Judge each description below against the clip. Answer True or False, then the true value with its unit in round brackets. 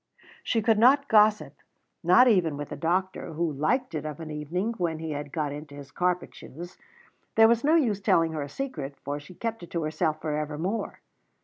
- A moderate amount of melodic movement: False (6.2 semitones)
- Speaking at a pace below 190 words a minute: False (205 wpm)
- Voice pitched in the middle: True (165 Hz)